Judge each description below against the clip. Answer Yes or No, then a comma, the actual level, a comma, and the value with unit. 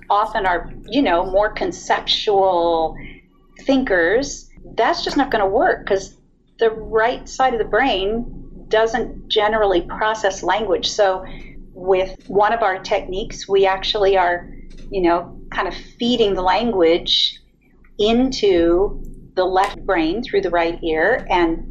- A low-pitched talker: No, high, 195 Hz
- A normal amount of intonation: Yes, average, 3.8 semitones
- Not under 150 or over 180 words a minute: No, slow, 135 wpm